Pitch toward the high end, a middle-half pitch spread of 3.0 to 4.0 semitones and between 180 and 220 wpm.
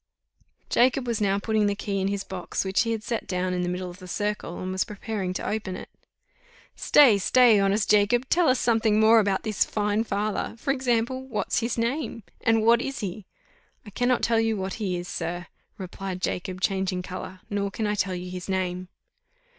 Yes: high, 205 Hz; average, 3.3 semitones; average, 200 wpm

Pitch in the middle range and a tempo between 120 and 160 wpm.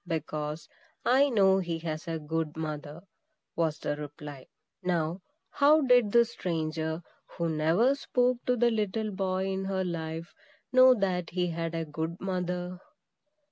Yes: medium, 175 Hz; average, 145 wpm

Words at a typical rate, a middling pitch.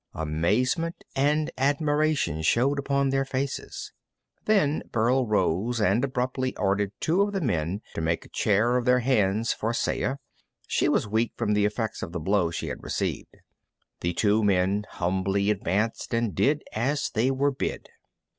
No: average, 160 wpm; low, 115 Hz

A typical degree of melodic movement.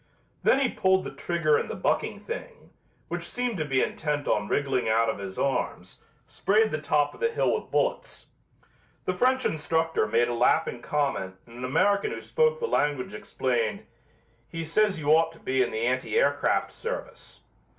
No: wide, 8.2 semitones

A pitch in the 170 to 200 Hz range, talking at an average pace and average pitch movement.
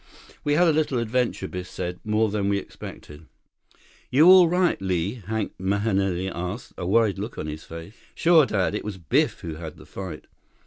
No: low, 100 Hz; average, 185 wpm; average, 4.7 semitones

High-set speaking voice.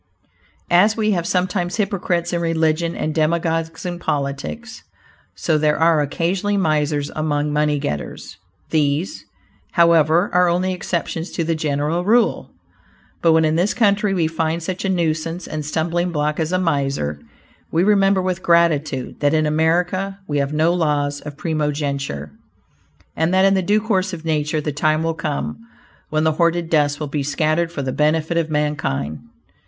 No: medium, 160 Hz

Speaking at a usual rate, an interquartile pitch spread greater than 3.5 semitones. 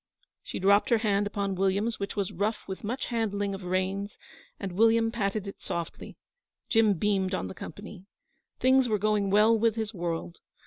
No: average, 175 wpm; narrow, 2.4 semitones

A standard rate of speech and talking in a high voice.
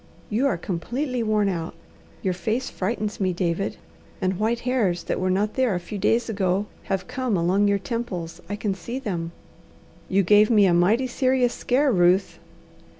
Yes: average, 175 wpm; high, 205 Hz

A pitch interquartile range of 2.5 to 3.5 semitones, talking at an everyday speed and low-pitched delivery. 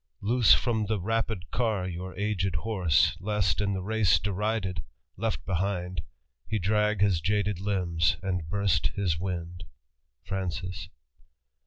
No: average, 2.9 semitones; slow, 130 wpm; very low, 95 Hz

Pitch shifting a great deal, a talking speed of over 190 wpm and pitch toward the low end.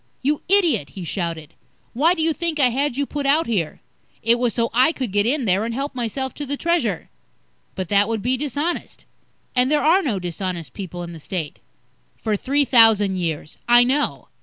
No: wide, 6.8 semitones; average, 200 wpm; high, 240 Hz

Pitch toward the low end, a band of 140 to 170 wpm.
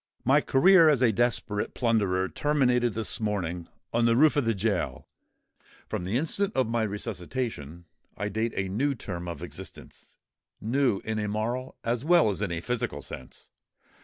Yes: low, 115 Hz; average, 160 wpm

